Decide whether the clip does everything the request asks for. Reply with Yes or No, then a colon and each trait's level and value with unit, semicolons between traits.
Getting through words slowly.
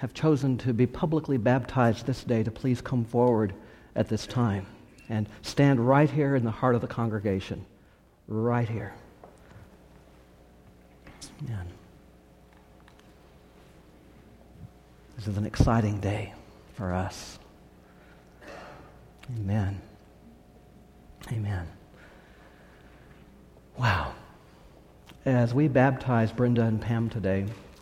Yes: slow, 95 wpm